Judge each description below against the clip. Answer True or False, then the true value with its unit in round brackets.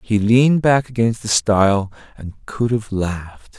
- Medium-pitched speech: False (110 Hz)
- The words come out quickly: False (165 wpm)